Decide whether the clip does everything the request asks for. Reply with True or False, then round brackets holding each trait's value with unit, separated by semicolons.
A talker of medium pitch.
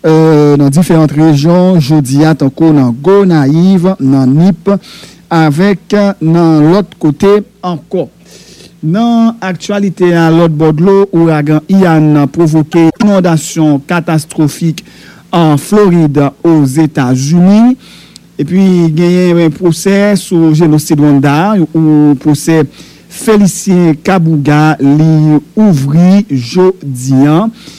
True (165 Hz)